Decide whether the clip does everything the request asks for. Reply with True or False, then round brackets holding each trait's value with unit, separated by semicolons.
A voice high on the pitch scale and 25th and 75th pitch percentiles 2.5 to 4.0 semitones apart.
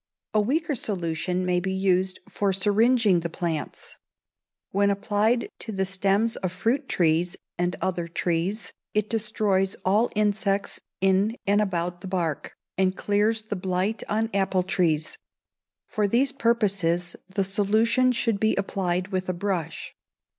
True (195 Hz; 2.9 semitones)